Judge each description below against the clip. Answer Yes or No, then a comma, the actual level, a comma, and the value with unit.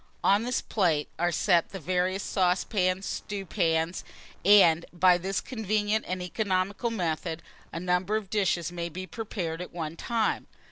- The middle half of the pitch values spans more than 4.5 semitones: No, average, 3.0 semitones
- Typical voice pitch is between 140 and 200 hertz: Yes, medium, 185 Hz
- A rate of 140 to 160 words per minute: Yes, average, 150 wpm